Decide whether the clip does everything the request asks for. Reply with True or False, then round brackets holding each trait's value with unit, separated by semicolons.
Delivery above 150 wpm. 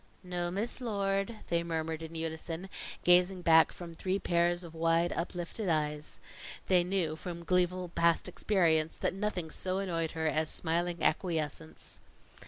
False (145 wpm)